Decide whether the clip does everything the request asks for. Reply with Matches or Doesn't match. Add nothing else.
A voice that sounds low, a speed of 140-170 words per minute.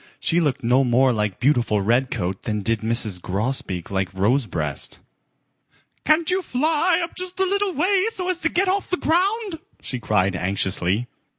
Matches